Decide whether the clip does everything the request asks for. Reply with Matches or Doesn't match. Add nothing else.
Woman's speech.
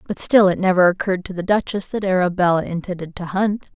Matches